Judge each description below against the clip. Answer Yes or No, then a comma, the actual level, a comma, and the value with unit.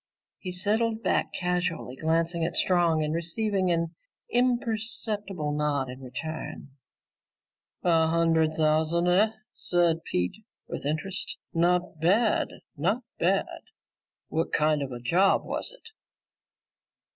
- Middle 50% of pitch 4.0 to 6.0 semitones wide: No, average, 3.6 semitones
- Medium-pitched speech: Yes, medium, 170 Hz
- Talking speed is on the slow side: Yes, slow, 115 wpm